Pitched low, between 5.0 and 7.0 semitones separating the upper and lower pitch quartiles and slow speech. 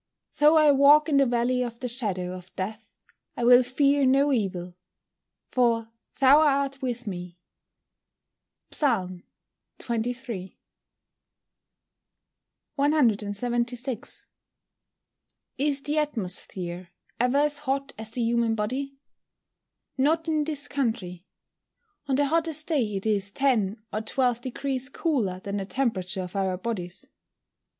No: high, 245 Hz; wide, 5.4 semitones; slow, 120 wpm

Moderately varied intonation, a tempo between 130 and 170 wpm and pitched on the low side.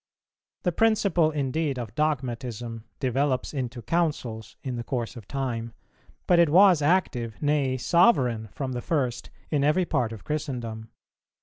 Yes: average, 4.7 semitones; average, 140 wpm; low, 130 Hz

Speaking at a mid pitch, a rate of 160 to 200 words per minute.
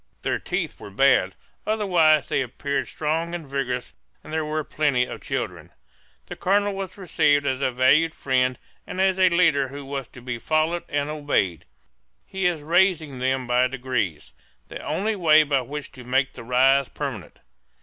Yes: medium, 145 Hz; average, 170 wpm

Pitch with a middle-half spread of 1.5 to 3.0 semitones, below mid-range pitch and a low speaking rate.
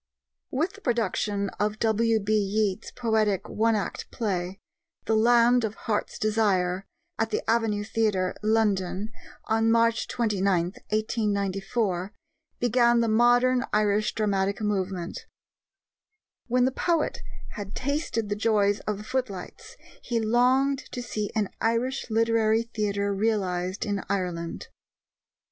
No: narrow, 2.4 semitones; high, 215 Hz; slow, 120 wpm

